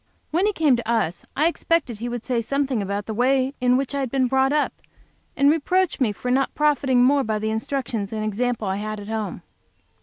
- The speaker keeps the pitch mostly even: No, average, 4.2 semitones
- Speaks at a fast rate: Yes, fast, 220 wpm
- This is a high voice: Yes, very high, 250 Hz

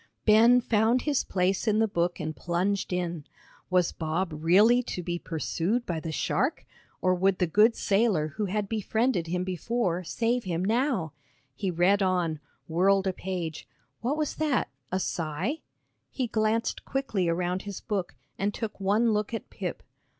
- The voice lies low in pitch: No, high, 190 Hz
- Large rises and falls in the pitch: No, average, 4.2 semitones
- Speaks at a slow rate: No, average, 165 wpm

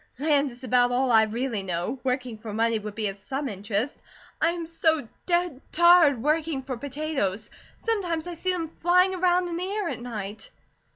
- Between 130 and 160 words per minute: No, average, 185 wpm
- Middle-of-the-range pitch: No, very high, 275 Hz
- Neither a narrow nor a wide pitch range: No, wide, 6.7 semitones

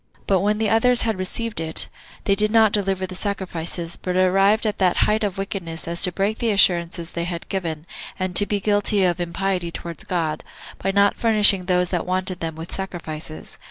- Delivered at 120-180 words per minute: No, average, 195 wpm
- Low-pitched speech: No, medium, 185 Hz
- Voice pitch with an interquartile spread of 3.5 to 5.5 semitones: No, average, 3.0 semitones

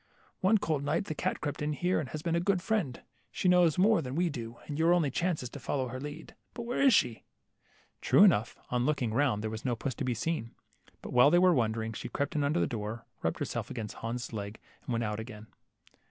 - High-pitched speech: No, medium, 140 Hz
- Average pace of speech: No, fast, 245 wpm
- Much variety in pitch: Yes, wide, 6.5 semitones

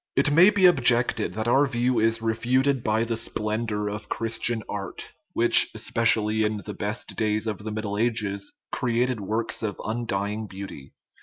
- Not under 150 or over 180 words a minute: Yes, average, 160 wpm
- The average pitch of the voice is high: No, low, 110 Hz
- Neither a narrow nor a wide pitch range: No, narrow, 2.1 semitones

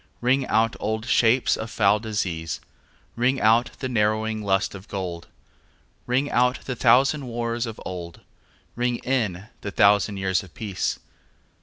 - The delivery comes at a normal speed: Yes, average, 145 wpm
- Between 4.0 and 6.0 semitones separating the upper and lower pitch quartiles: No, average, 3.6 semitones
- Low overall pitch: Yes, low, 110 Hz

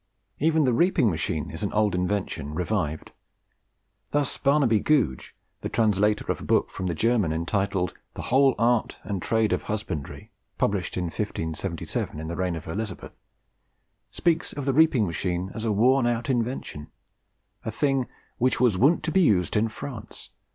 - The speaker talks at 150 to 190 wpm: Yes, average, 165 wpm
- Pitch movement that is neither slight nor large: No, wide, 6.1 semitones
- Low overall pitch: Yes, low, 105 Hz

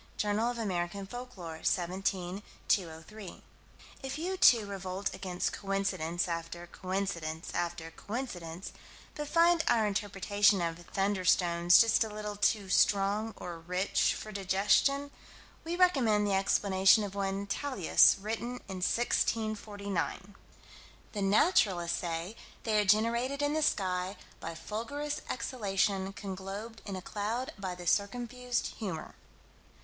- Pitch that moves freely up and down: No, average, 3.6 semitones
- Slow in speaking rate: Yes, slow, 125 wpm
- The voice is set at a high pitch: Yes, high, 200 Hz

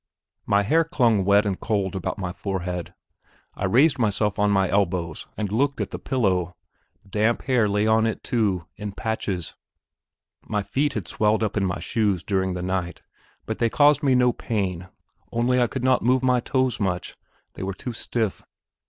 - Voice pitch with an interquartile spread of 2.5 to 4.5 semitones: Yes, average, 4.2 semitones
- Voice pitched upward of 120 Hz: No, low, 105 Hz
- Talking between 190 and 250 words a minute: No, average, 180 wpm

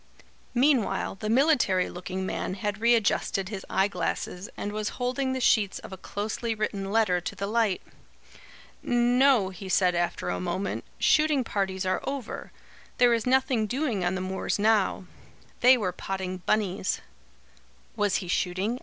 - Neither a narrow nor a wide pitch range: Yes, average, 4.2 semitones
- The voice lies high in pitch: Yes, high, 205 Hz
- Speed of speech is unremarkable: Yes, average, 155 wpm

